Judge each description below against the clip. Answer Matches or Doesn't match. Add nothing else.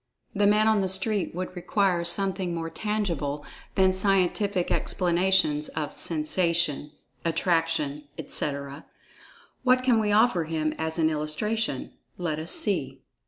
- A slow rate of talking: Matches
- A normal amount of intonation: Matches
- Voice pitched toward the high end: Doesn't match